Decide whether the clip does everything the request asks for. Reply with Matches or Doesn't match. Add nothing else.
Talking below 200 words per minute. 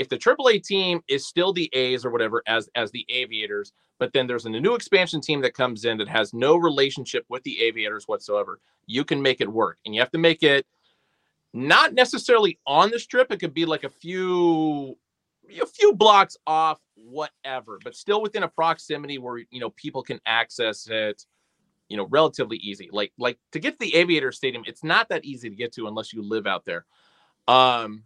Doesn't match